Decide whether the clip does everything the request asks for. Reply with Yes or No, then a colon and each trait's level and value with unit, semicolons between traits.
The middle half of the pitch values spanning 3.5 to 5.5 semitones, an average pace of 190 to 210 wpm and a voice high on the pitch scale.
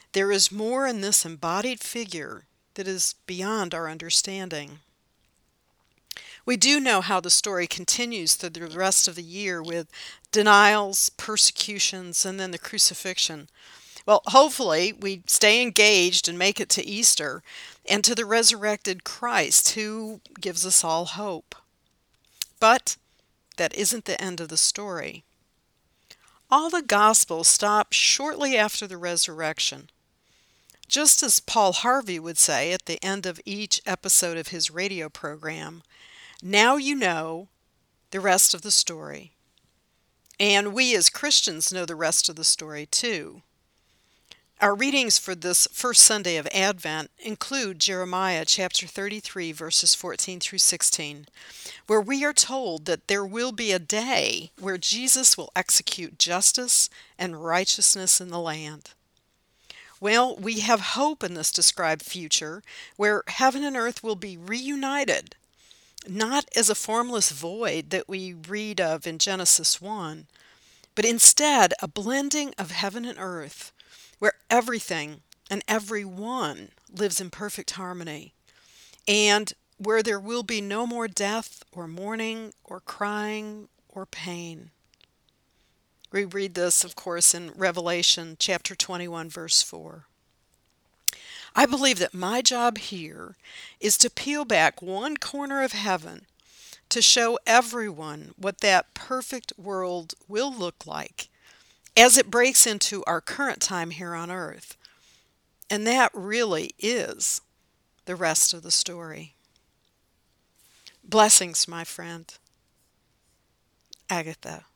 No: average, 4.4 semitones; slow, 135 wpm; high, 195 Hz